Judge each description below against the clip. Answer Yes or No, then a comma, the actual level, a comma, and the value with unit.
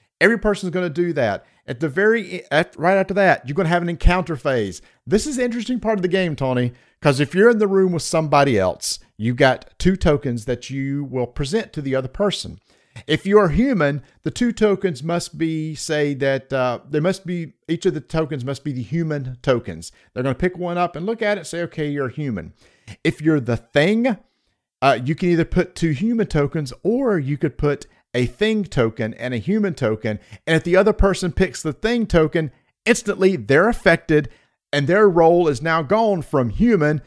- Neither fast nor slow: No, fast, 210 wpm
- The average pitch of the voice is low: No, medium, 160 Hz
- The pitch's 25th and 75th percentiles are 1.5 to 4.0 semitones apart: No, wide, 5.6 semitones